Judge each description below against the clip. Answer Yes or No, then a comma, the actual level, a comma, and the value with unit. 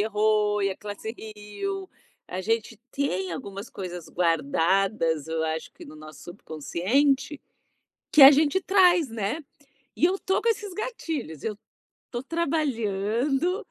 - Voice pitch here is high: Yes, high, 220 Hz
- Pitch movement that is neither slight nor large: No, wide, 8.3 semitones